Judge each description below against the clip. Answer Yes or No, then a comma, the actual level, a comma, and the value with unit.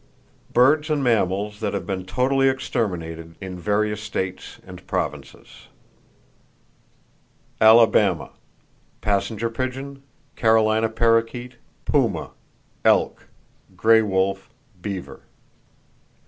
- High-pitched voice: No, low, 110 Hz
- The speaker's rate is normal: No, slow, 85 wpm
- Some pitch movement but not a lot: Yes, average, 4.0 semitones